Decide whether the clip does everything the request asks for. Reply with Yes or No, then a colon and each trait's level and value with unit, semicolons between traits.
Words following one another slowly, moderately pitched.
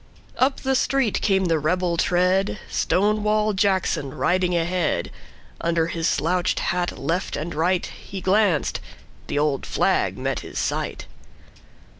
Yes: slow, 115 wpm; medium, 180 Hz